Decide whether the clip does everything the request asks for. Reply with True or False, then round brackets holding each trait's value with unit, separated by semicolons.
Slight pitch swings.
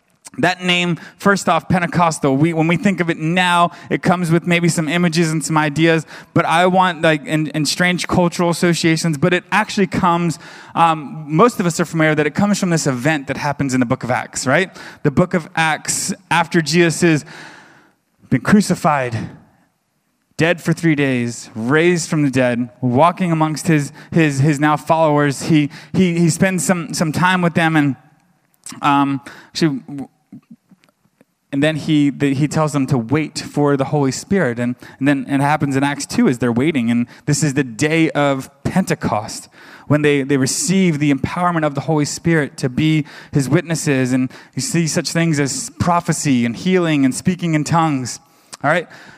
False (3.4 semitones)